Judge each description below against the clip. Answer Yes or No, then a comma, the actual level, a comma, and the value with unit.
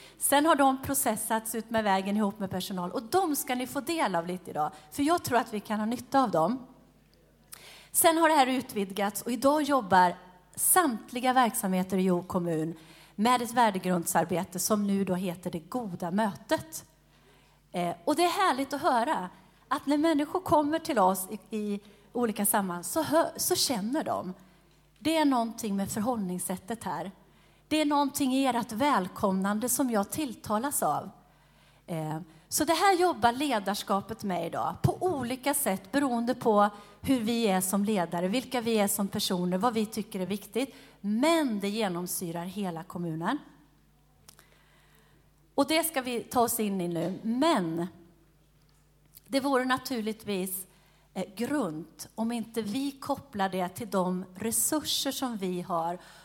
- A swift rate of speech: No, average, 155 wpm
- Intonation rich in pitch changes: Yes, wide, 6.4 semitones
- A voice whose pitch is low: No, high, 215 Hz